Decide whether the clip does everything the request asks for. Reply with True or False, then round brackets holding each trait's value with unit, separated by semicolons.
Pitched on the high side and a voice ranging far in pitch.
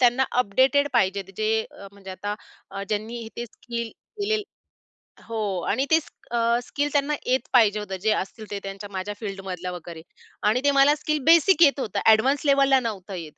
True (230 Hz; 5.7 semitones)